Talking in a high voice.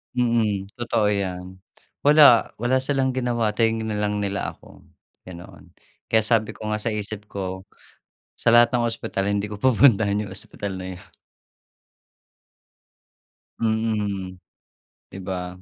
No: low, 105 Hz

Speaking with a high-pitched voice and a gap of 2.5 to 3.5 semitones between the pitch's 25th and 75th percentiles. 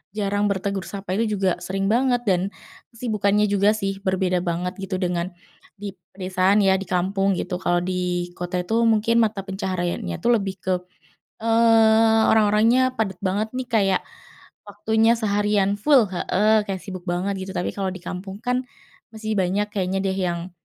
Yes: high, 195 Hz; average, 2.8 semitones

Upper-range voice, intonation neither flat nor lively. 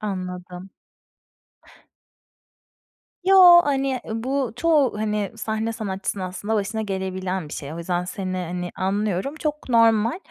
Yes: high, 210 Hz; average, 4.6 semitones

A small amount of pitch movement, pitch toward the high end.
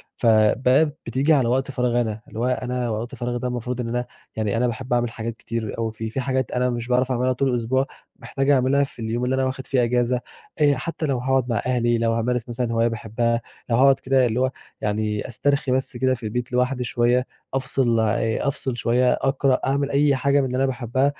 No: narrow, 2.1 semitones; low, 125 Hz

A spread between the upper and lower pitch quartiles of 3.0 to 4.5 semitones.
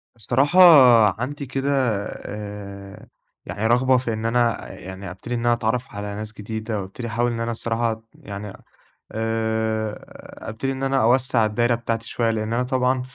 No: narrow, 2.4 semitones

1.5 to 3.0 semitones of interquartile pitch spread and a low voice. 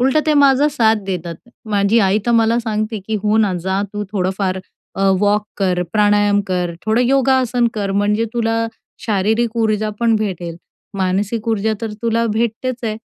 No: narrow, 2.6 semitones; high, 215 Hz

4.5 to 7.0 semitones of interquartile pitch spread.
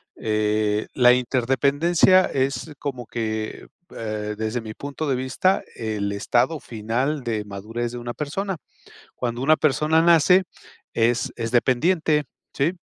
Yes: average, 5.3 semitones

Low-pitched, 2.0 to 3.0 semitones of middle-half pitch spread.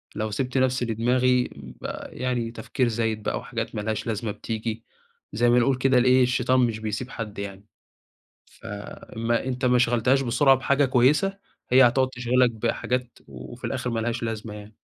Yes: low, 120 Hz; narrow, 2.5 semitones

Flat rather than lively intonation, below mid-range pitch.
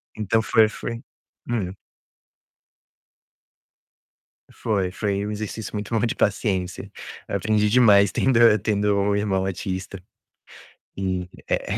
Yes: narrow, 2.1 semitones; low, 105 Hz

